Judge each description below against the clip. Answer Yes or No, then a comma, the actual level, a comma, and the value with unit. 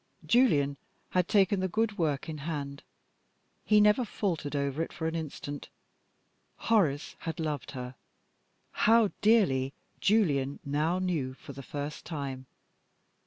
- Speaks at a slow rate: Yes, slow, 130 wpm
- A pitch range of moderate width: No, wide, 6.0 semitones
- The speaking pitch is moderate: Yes, medium, 155 Hz